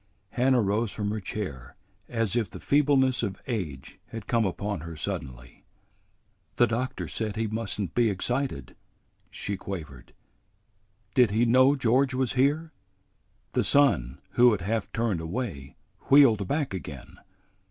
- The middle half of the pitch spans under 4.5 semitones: No, average, 5.3 semitones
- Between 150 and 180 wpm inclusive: No, average, 140 wpm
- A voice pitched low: Yes, low, 110 Hz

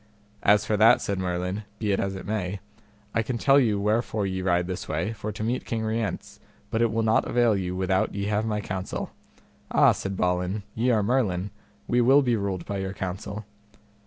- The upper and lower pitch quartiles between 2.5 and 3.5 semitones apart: Yes, average, 2.9 semitones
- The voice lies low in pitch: Yes, low, 105 Hz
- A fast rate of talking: Yes, fast, 210 wpm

